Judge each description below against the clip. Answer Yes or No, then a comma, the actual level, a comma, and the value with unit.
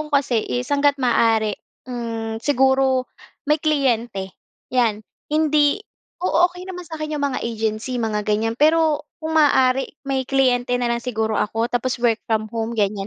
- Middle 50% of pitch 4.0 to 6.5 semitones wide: Yes, average, 4.4 semitones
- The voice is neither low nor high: No, very high, 250 Hz